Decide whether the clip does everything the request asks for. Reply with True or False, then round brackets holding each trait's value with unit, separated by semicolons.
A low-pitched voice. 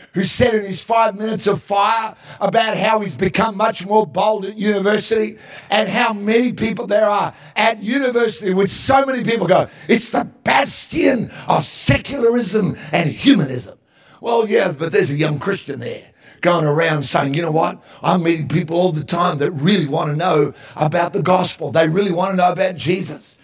False (195 Hz)